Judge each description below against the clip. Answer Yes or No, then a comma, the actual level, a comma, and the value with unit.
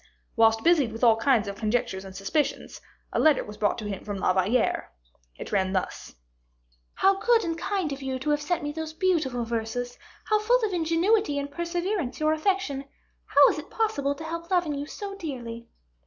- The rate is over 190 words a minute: Yes, average, 200 wpm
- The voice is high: Yes, very high, 285 Hz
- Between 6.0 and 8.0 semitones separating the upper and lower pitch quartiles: Yes, wide, 7.1 semitones